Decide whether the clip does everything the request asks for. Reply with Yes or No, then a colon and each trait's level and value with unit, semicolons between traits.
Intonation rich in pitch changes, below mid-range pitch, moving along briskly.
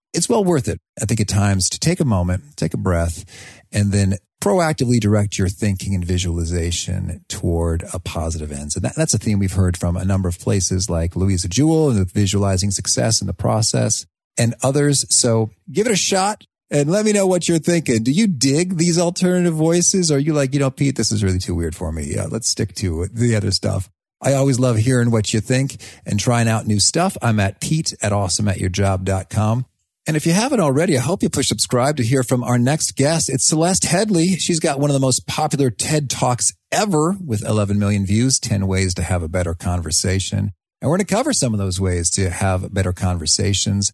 Yes: wide, 6.7 semitones; low, 110 Hz; fast, 220 wpm